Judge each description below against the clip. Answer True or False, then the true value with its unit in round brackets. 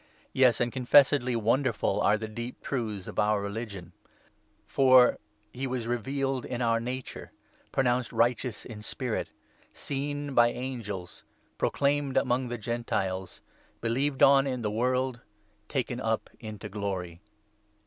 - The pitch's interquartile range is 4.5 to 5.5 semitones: False (3.5 semitones)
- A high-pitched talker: False (120 Hz)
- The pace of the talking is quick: False (140 wpm)